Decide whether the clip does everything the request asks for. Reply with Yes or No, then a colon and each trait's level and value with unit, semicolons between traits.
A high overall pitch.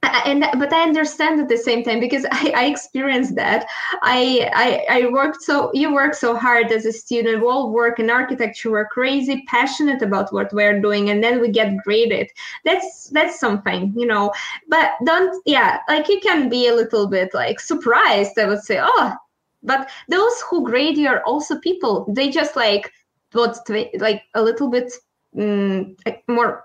Yes: high, 245 Hz